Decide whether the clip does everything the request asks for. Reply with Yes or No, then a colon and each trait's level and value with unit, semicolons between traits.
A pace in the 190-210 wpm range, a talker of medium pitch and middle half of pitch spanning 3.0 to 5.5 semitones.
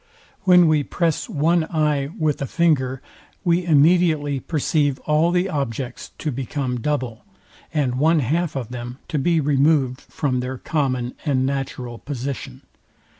No: average, 140 wpm; medium, 145 Hz; average, 3.5 semitones